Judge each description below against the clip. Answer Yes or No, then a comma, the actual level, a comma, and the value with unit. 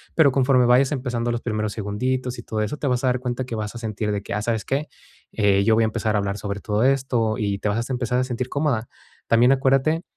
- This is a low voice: Yes, low, 120 Hz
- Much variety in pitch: No, average, 3.2 semitones